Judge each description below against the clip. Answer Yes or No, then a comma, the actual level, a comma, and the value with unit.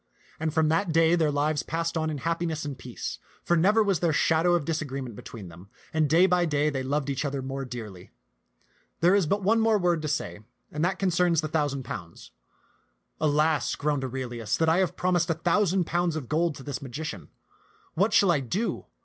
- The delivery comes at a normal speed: No, fast, 215 wpm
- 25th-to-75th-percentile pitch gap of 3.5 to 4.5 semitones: Yes, average, 4.0 semitones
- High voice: No, medium, 155 Hz